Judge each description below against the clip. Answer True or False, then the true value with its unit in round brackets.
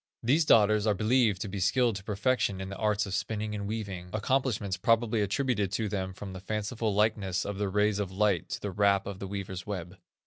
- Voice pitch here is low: True (105 Hz)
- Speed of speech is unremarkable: False (215 wpm)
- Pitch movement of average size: False (1.9 semitones)